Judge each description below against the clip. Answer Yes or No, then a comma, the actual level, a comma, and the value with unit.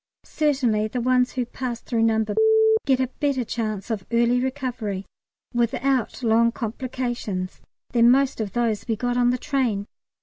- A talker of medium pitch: No, high, 240 Hz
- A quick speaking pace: No, average, 155 wpm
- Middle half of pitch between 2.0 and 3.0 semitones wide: Yes, narrow, 2.5 semitones